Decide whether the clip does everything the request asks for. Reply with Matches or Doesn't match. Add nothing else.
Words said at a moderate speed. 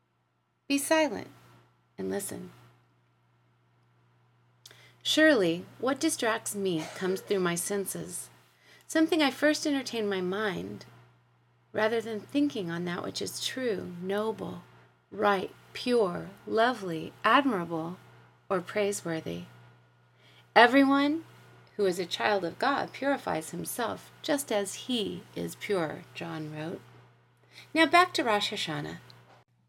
Doesn't match